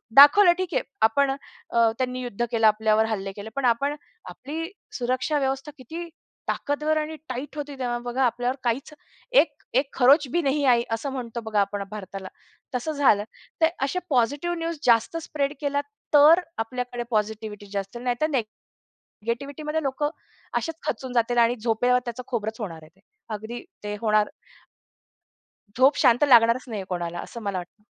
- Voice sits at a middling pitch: No, high, 245 Hz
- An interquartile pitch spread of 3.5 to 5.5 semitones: Yes, average, 4.5 semitones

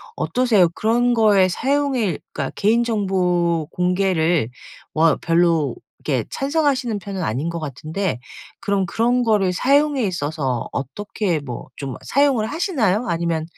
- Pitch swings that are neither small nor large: No, wide, 6.3 semitones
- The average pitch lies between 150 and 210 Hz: Yes, high, 190 Hz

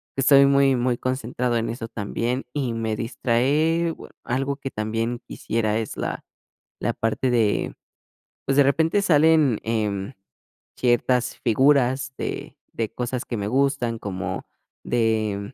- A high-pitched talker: No, low, 120 Hz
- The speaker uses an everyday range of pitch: Yes, average, 3.3 semitones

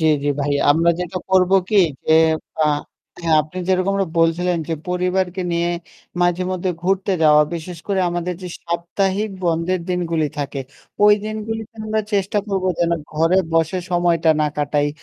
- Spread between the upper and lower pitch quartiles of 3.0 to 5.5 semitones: No, narrow, 2.4 semitones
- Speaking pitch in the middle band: Yes, medium, 175 Hz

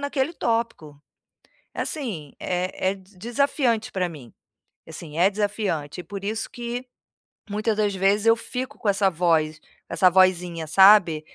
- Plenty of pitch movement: No, average, 4.8 semitones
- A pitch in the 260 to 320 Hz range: No, high, 195 Hz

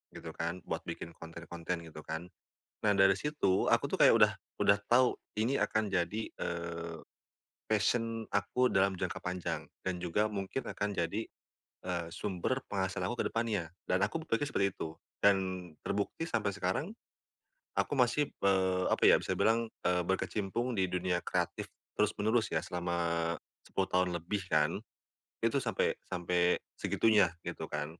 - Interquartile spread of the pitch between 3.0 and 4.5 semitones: Yes, average, 3.8 semitones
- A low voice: Yes, very low, 95 Hz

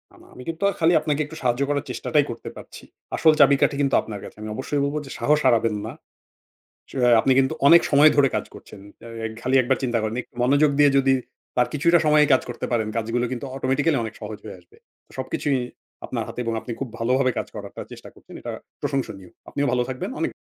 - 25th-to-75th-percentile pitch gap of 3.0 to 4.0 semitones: Yes, average, 3.5 semitones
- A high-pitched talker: No, low, 135 Hz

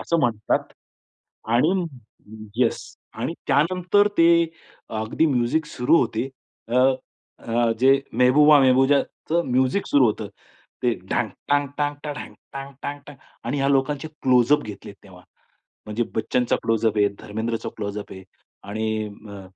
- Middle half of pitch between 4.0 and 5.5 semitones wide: Yes, average, 4.6 semitones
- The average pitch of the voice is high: No, low, 125 Hz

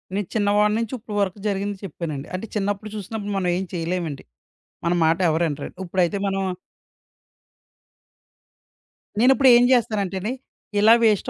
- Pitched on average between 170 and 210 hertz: Yes, high, 200 Hz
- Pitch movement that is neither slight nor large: Yes, average, 3.0 semitones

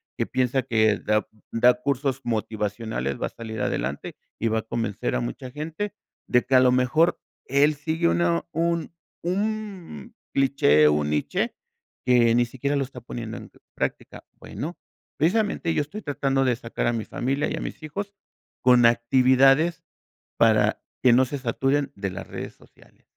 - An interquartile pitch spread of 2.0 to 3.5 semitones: No, average, 4.8 semitones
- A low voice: Yes, low, 130 Hz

